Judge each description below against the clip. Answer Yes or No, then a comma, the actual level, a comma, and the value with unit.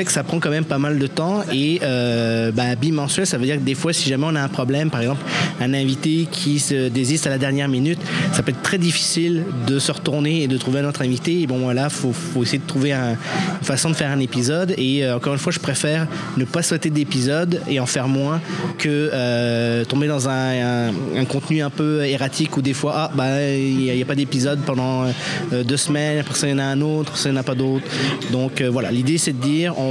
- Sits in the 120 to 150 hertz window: Yes, medium, 140 Hz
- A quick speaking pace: Yes, fast, 260 wpm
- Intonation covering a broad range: No, average, 3.1 semitones